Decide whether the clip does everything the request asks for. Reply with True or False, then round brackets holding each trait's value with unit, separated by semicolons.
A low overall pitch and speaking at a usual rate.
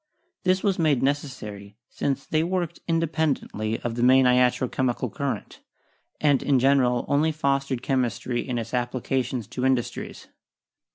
True (130 Hz; 145 wpm)